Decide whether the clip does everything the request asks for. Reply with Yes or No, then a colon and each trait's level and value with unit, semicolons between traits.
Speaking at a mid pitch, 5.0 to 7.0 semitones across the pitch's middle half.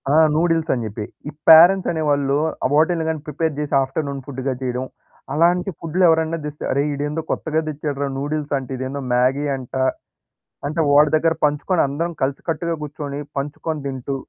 No: medium, 150 Hz; narrow, 2.6 semitones